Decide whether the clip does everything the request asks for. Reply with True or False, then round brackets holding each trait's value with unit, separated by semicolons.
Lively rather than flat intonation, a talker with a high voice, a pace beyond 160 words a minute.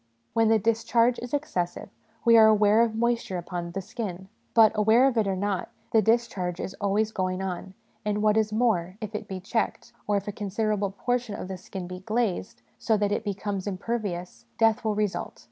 False (2.9 semitones; 210 Hz; 200 wpm)